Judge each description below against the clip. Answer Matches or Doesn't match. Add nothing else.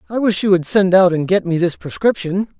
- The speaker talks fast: Matches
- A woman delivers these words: Doesn't match